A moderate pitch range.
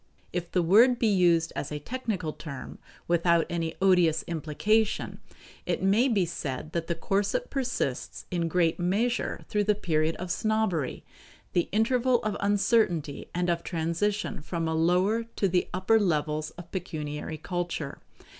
Yes: average, 4.4 semitones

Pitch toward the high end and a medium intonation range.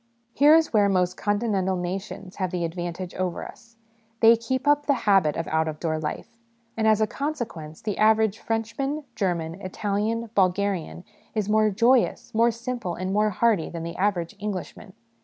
Yes: high, 205 Hz; average, 4.2 semitones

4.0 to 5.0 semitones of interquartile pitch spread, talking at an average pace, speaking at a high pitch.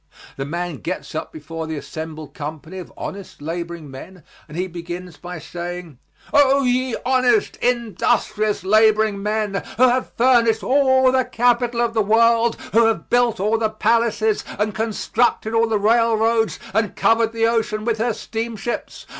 Yes: average, 4.6 semitones; average, 155 wpm; high, 220 Hz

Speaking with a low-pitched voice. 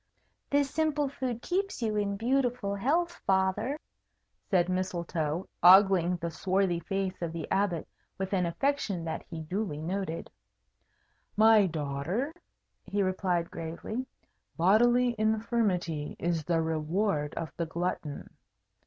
No: high, 190 Hz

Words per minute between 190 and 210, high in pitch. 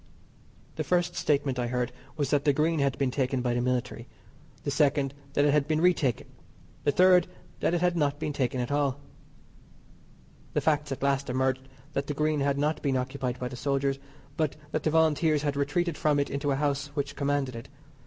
No: fast, 205 wpm; medium, 140 Hz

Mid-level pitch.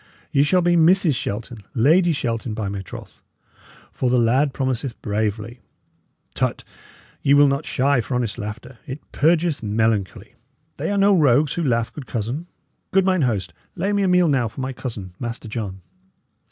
No: low, 125 Hz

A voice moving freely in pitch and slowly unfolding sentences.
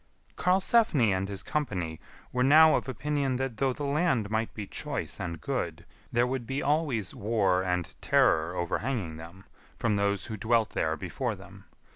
No: wide, 6.4 semitones; average, 165 wpm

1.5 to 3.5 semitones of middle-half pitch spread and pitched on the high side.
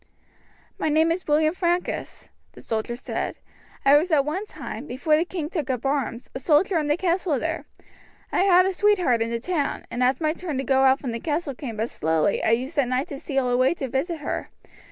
No: average, 4.7 semitones; very high, 290 Hz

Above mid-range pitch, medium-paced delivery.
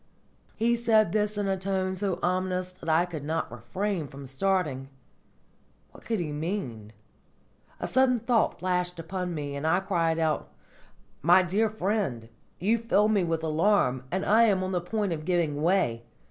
No: medium, 180 Hz; average, 170 wpm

